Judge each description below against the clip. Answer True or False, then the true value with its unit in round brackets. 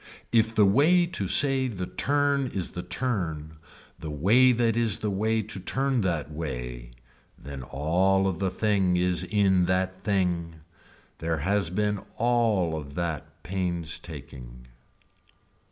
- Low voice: True (95 Hz)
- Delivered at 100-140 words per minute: True (135 wpm)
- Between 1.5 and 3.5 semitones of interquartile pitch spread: False (5.2 semitones)